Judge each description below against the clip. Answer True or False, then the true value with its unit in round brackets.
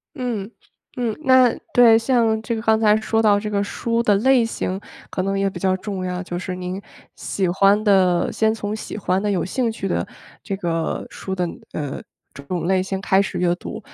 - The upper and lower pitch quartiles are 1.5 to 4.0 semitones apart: True (3.3 semitones)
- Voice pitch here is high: True (200 Hz)